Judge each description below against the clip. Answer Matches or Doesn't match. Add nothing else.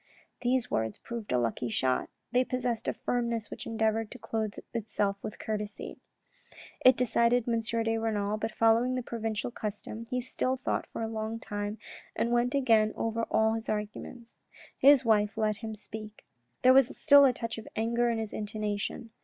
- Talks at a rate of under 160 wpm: Doesn't match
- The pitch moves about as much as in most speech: Doesn't match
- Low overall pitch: Doesn't match